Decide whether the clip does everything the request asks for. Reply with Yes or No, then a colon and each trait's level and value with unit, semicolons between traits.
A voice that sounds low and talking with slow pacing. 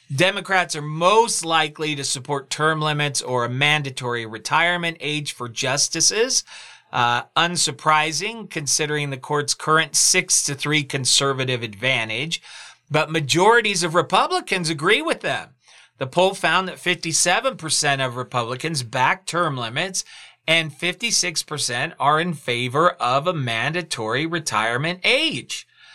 No: medium, 155 Hz; slow, 125 wpm